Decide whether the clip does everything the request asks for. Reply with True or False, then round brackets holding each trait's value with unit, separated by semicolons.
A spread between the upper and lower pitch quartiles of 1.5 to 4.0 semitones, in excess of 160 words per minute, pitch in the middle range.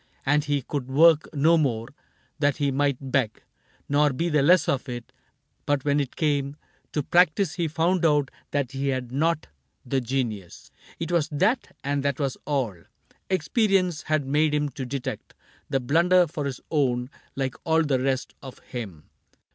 True (3.0 semitones; 170 wpm; 145 Hz)